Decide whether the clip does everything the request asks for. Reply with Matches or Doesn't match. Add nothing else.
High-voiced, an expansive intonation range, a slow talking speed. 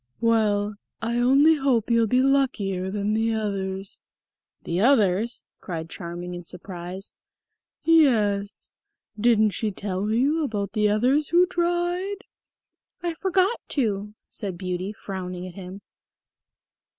Matches